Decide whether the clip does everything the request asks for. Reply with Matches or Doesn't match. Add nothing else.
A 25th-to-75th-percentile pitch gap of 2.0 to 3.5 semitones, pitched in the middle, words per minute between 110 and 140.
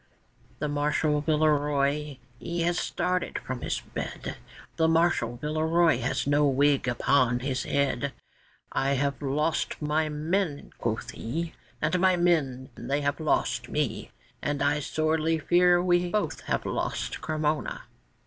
Matches